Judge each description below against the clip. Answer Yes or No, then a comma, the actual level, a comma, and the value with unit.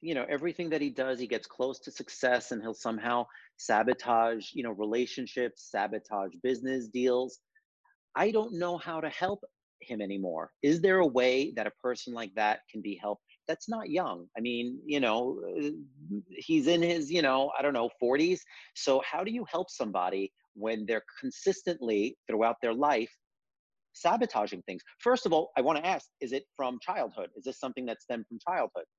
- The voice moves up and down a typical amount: No, wide, 6.7 semitones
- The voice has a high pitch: No, low, 130 Hz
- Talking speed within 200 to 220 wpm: No, average, 185 wpm